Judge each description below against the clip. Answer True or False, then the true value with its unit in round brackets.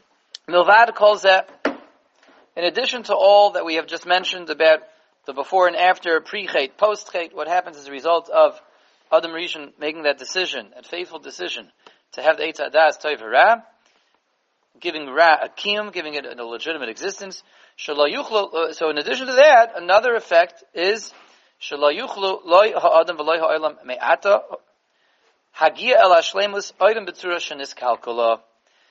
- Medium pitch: True (170 Hz)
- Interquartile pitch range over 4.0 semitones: True (4.6 semitones)